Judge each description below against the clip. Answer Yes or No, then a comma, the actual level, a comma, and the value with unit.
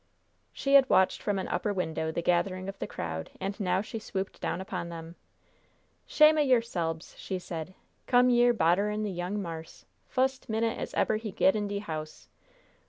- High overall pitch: Yes, high, 195 Hz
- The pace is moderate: Yes, average, 180 wpm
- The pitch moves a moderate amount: Yes, average, 4.5 semitones